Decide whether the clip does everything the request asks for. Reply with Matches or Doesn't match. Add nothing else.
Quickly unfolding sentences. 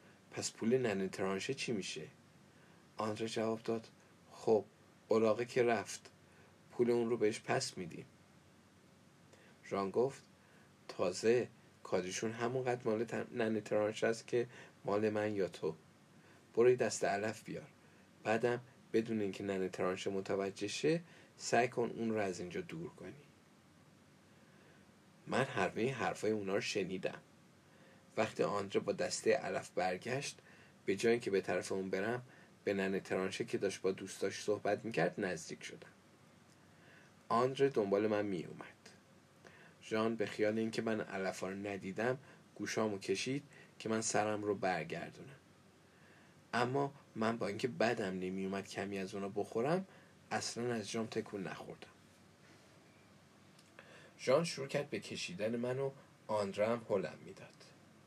Doesn't match